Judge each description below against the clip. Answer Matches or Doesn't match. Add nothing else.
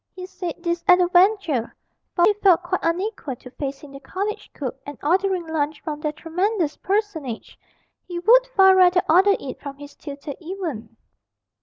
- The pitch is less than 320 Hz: Doesn't match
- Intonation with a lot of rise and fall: Doesn't match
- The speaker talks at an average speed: Matches